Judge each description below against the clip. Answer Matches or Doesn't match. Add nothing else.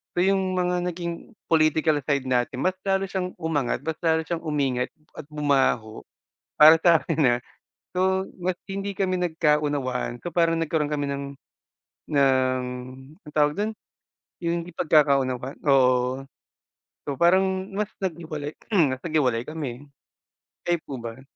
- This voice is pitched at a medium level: Matches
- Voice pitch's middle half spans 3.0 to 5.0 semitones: Matches